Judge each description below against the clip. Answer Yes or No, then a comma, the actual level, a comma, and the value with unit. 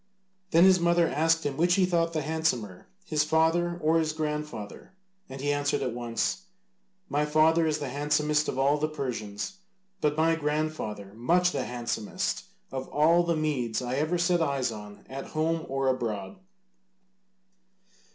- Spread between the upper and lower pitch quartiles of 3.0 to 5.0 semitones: Yes, average, 3.7 semitones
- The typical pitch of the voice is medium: Yes, medium, 150 Hz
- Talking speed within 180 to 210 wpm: No, average, 160 wpm